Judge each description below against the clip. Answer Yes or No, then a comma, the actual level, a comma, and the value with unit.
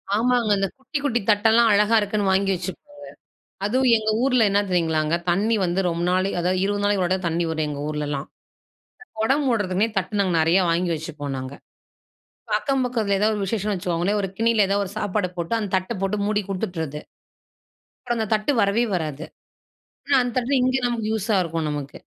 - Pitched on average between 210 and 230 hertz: No, high, 200 Hz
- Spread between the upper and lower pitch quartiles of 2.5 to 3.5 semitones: No, average, 4.4 semitones